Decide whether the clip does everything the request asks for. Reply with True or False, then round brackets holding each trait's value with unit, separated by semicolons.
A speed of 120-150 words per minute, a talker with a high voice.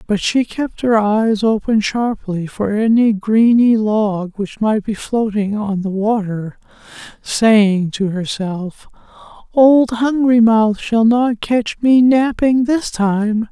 True (140 wpm; 220 Hz)